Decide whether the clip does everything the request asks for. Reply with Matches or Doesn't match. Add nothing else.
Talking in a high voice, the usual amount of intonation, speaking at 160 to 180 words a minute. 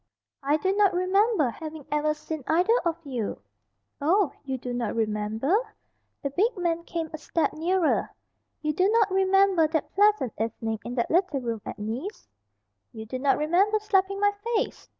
Doesn't match